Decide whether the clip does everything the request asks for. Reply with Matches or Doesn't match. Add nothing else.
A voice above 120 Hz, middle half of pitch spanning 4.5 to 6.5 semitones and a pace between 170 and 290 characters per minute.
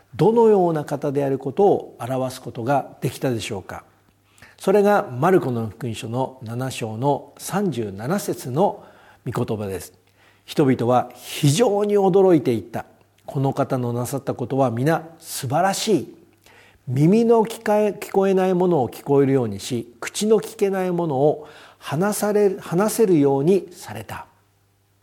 Doesn't match